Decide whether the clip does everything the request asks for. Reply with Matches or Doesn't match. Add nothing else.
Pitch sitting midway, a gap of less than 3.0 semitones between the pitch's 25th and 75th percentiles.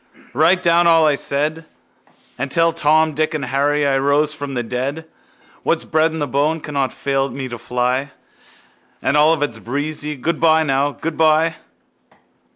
Matches